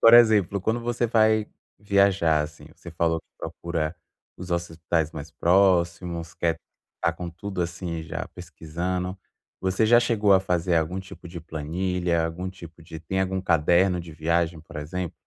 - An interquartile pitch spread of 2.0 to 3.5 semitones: Yes, narrow, 2.5 semitones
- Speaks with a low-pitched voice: Yes, very low, 85 Hz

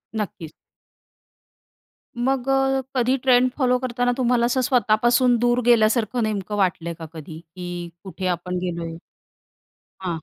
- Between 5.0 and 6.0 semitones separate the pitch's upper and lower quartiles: Yes, wide, 5.6 semitones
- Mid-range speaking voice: No, high, 235 Hz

